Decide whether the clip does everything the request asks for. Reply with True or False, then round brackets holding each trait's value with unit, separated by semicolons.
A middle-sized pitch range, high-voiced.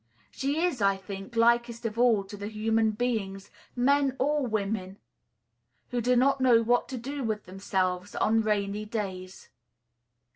True (3.7 semitones; 225 Hz)